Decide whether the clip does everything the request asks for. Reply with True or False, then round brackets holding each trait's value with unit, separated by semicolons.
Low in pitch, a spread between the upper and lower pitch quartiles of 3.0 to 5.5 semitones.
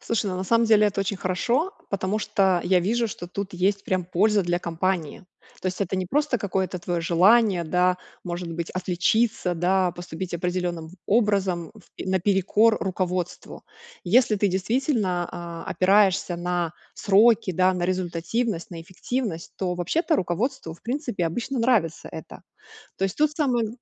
False (185 Hz; 3.6 semitones)